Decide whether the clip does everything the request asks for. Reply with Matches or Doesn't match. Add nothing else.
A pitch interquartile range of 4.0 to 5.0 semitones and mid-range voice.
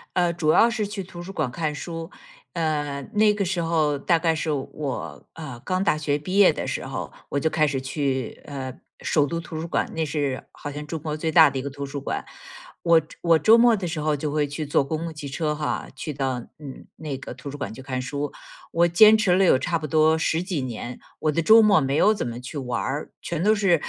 Doesn't match